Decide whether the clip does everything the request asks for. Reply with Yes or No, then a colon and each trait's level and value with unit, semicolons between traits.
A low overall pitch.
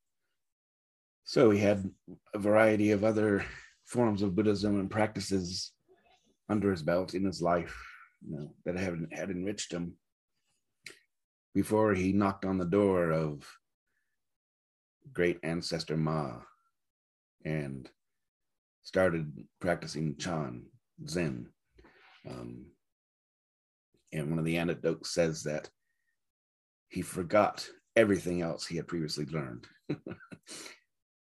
Yes: very low, 85 Hz